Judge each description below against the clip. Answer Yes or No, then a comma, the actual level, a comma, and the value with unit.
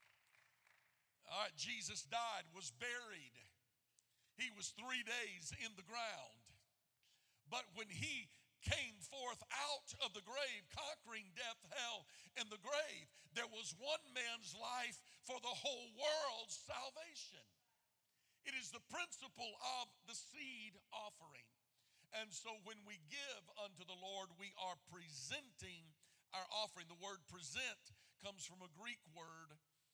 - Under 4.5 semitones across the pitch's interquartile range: No, wide, 5.4 semitones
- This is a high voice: Yes, high, 215 Hz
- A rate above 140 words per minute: No, slow, 135 wpm